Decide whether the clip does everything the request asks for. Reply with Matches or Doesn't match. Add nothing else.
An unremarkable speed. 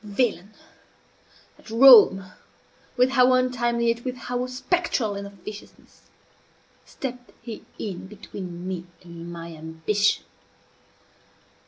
Doesn't match